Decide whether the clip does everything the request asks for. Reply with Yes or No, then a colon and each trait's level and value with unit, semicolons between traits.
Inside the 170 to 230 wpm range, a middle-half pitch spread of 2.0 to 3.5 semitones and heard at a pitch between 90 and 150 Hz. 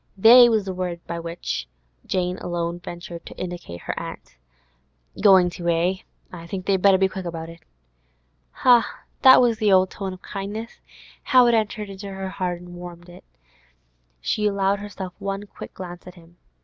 No: average, 175 wpm; narrow, 2.5 semitones; medium, 185 Hz